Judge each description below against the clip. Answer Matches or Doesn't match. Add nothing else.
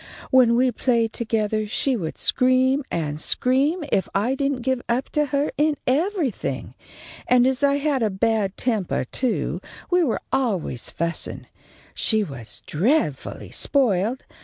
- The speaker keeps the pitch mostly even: Doesn't match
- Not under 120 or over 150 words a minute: Matches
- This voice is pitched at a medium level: Doesn't match